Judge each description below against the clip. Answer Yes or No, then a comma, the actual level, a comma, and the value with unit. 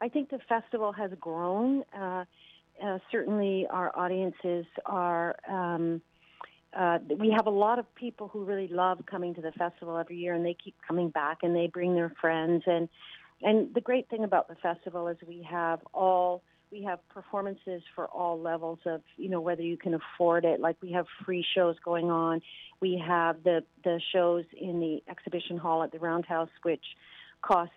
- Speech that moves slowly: No, average, 185 wpm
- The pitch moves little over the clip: Yes, narrow, 2.0 semitones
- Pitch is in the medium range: Yes, medium, 175 Hz